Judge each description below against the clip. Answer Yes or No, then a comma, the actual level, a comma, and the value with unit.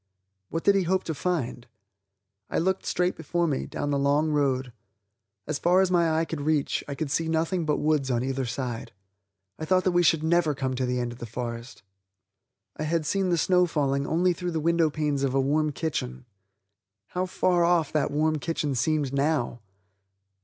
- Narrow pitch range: No, average, 3.7 semitones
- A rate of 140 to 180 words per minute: No, average, 195 wpm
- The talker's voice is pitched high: No, medium, 155 Hz